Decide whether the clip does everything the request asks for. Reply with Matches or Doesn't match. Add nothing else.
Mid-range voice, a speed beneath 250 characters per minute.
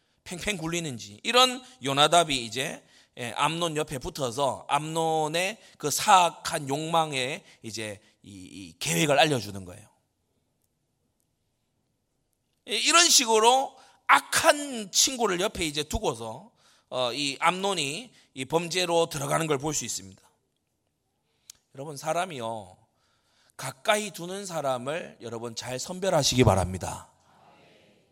Matches